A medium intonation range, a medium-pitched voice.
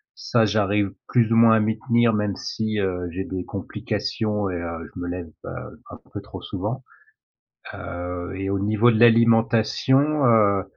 No: average, 3.4 semitones; low, 105 Hz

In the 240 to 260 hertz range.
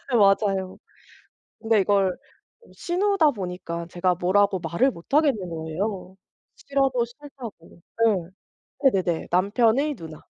No: high, 200 Hz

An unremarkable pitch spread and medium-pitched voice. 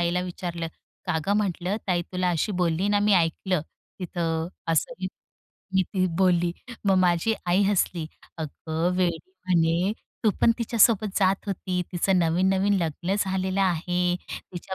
No: narrow, 1.9 semitones; medium, 180 Hz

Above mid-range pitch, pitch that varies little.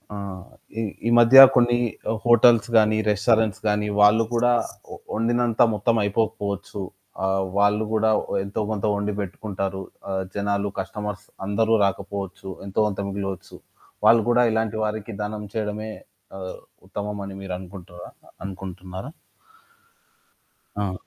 No: low, 105 Hz; narrow, 2.2 semitones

